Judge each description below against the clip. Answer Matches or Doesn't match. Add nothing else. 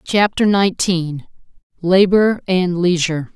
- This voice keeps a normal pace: Doesn't match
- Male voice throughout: Doesn't match